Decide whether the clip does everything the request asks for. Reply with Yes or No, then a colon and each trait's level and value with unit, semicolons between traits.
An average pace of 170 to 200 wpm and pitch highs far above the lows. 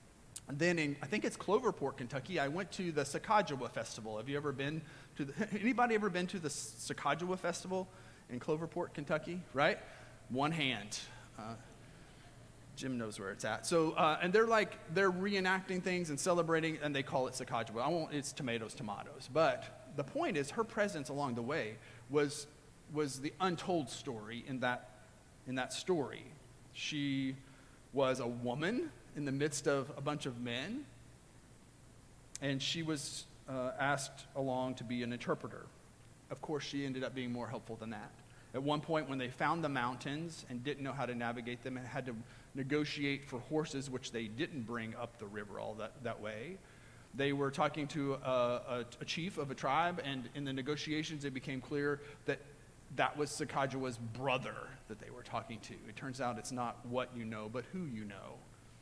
No: average, 185 wpm; average, 3.8 semitones